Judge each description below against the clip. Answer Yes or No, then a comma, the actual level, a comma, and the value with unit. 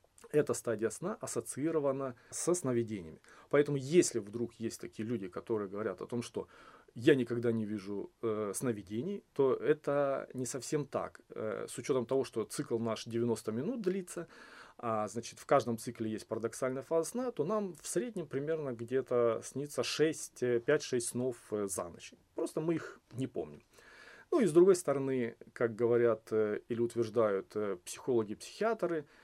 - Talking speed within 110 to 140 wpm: No, average, 155 wpm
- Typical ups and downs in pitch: Yes, average, 4.6 semitones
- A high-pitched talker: No, low, 125 Hz